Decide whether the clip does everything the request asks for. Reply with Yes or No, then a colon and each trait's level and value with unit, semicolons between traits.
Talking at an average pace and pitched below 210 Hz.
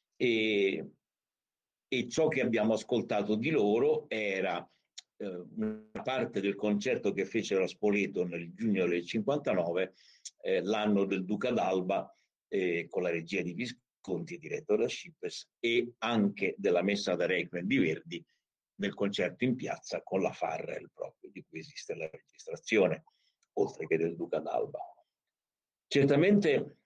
Yes: average, 140 wpm; medium, 140 Hz